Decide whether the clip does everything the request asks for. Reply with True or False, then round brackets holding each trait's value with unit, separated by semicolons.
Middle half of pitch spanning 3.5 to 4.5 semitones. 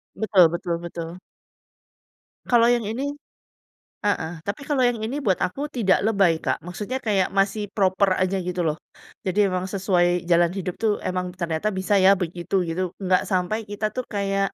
False (3.1 semitones)